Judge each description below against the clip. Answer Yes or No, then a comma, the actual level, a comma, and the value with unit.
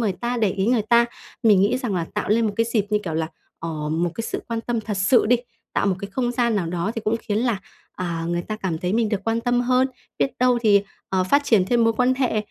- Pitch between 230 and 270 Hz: No, high, 215 Hz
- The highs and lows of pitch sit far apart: No, average, 4.0 semitones